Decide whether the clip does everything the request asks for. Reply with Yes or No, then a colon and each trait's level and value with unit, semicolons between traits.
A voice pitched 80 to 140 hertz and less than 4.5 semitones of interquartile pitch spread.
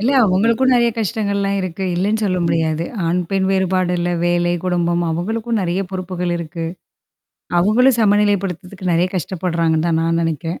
No: medium, 185 Hz; average, 2.8 semitones